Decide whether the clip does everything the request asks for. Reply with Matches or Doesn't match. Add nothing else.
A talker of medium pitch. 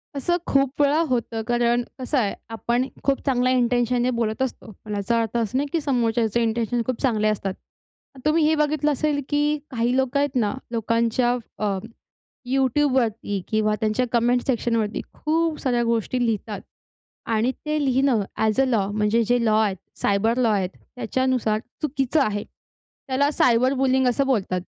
Doesn't match